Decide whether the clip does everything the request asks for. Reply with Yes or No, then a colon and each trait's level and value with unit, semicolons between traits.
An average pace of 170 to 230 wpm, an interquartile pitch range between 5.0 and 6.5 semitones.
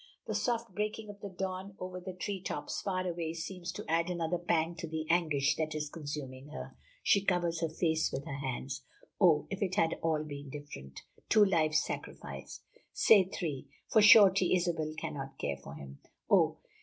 No: average, 180 wpm; average, 3.9 semitones